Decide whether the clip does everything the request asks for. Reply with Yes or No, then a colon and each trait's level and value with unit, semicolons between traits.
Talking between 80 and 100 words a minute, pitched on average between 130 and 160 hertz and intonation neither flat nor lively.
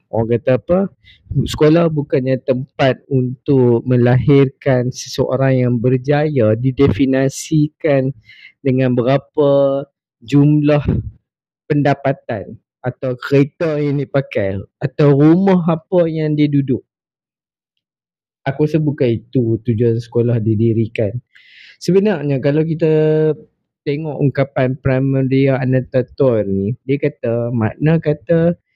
Yes: average, 95 wpm; low, 135 Hz; average, 3.0 semitones